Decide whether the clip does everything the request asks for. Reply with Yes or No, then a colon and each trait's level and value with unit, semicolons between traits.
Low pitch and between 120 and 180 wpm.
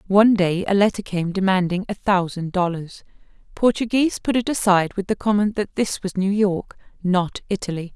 No: high, 195 Hz; average, 175 wpm